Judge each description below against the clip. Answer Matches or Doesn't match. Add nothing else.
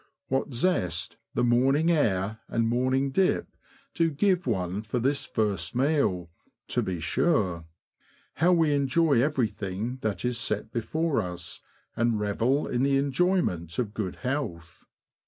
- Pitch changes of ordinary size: Doesn't match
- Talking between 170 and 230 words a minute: Doesn't match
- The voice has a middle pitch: Doesn't match